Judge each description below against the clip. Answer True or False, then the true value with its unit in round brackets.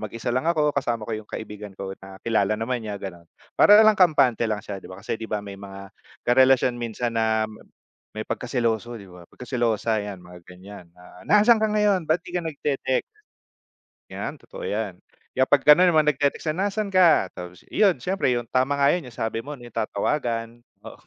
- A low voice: True (120 Hz)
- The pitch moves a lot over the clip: True (6.2 semitones)